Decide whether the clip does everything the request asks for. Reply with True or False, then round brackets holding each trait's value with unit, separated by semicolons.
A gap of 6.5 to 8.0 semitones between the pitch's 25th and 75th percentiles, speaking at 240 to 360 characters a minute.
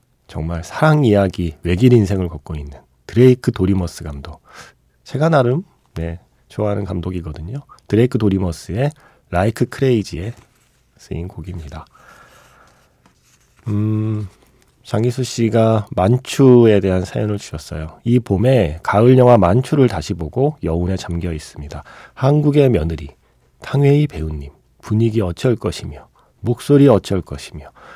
True (6.8 semitones; 295 characters per minute)